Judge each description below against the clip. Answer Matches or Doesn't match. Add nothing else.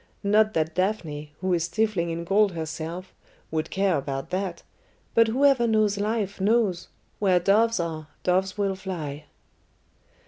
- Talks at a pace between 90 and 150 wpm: Matches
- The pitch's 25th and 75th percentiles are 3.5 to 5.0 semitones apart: Matches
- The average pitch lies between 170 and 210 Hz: Matches